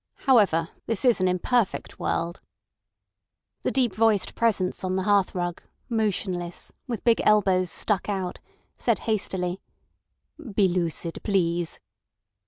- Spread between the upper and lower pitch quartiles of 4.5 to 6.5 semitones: No, average, 3.4 semitones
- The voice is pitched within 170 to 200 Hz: Yes, high, 190 Hz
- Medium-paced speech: No, slow, 115 wpm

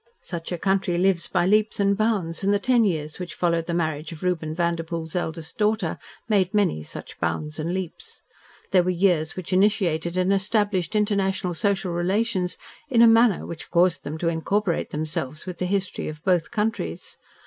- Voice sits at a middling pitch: Yes, medium, 180 Hz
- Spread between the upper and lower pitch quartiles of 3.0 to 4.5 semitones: Yes, average, 3.4 semitones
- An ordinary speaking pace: Yes, average, 180 wpm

